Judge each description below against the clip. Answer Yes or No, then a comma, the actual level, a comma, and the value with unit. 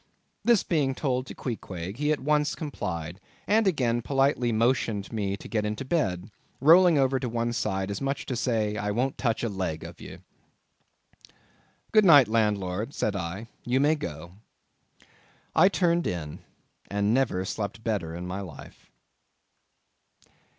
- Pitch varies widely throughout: Yes, wide, 5.7 semitones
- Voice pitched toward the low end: Yes, low, 115 Hz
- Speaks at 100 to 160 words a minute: Yes, average, 150 wpm